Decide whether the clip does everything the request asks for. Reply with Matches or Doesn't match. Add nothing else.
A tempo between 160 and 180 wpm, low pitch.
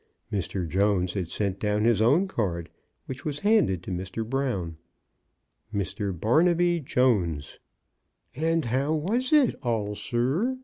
Doesn't match